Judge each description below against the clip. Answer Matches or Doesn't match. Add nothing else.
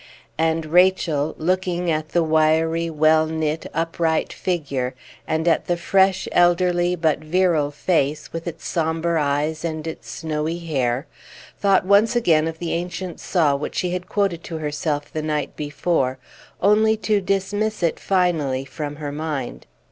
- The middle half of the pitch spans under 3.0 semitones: Matches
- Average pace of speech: Matches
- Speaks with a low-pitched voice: Doesn't match